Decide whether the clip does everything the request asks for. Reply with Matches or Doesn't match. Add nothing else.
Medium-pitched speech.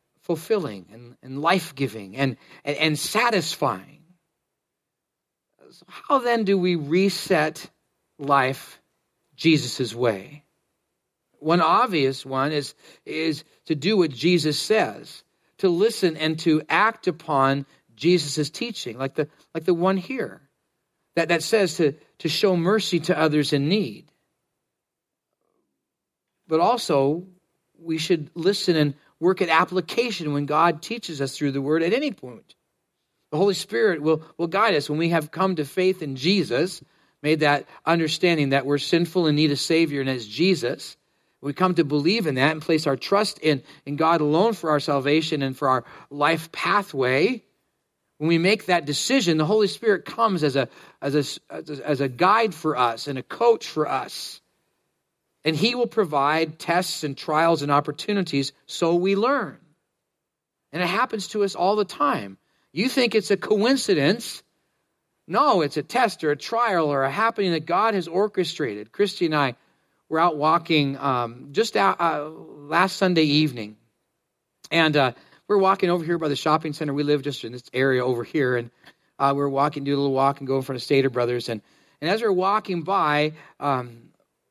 Matches